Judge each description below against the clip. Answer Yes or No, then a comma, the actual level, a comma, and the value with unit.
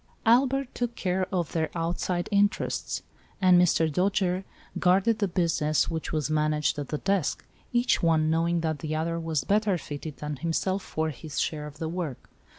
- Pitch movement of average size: Yes, average, 3.5 semitones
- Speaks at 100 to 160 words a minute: No, average, 170 wpm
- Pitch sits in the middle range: Yes, medium, 170 Hz